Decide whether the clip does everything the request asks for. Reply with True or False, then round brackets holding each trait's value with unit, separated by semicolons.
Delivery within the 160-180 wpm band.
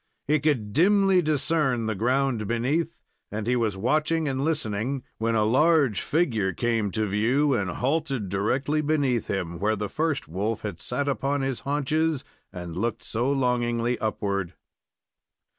False (150 wpm)